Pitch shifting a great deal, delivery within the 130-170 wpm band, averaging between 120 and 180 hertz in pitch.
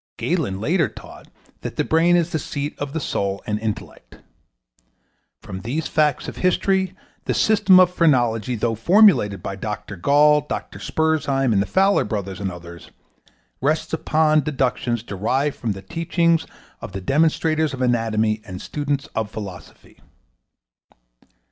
Yes: wide, 7.1 semitones; average, 140 wpm; low, 135 Hz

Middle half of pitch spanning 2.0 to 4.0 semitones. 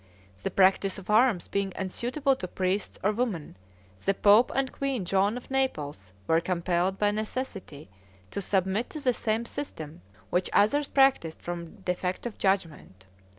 No: average, 5.1 semitones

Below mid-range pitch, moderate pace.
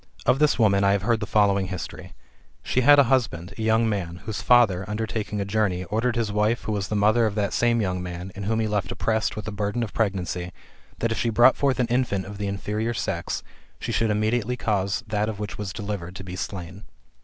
No: low, 105 Hz; fast, 235 wpm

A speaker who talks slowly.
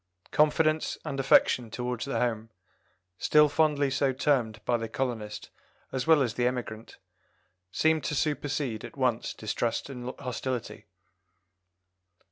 Yes: slow, 125 wpm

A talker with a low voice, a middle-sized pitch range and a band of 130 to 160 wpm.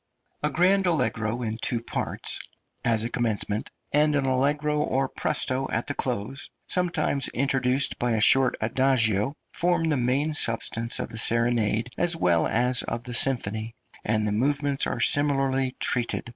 Yes: low, 130 Hz; average, 3.8 semitones; average, 155 wpm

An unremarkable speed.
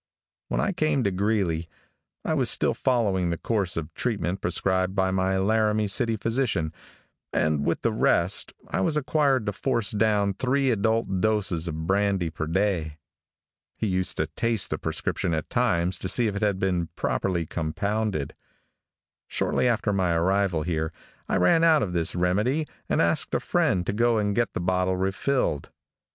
Yes: average, 170 wpm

